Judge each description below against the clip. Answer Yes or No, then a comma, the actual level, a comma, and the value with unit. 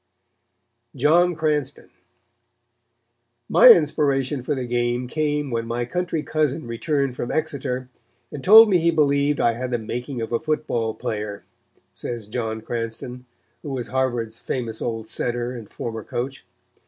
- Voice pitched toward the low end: Yes, low, 125 Hz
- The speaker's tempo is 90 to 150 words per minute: Yes, average, 140 wpm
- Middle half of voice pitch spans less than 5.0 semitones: Yes, average, 4.1 semitones